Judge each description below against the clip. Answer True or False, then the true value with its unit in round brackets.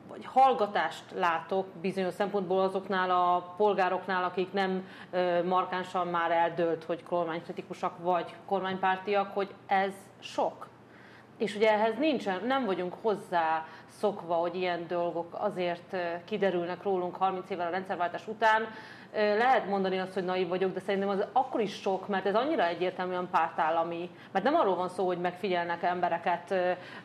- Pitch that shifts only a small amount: True (2.1 semitones)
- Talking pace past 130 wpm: True (140 wpm)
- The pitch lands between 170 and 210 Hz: True (185 Hz)